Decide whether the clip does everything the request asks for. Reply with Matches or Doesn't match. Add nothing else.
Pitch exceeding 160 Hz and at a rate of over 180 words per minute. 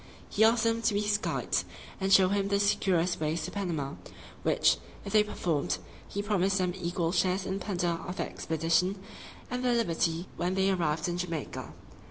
Matches